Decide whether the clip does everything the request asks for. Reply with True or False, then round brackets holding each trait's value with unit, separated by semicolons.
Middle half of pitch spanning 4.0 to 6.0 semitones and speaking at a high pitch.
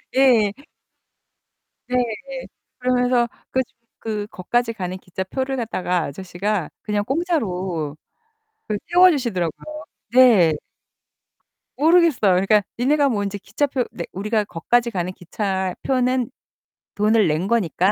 True (5.3 semitones; 215 Hz)